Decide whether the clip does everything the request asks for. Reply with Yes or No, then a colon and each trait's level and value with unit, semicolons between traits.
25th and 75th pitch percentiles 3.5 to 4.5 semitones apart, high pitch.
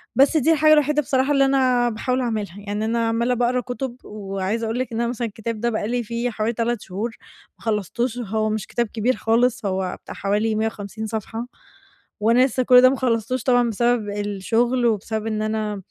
No: narrow, 2.5 semitones; high, 230 Hz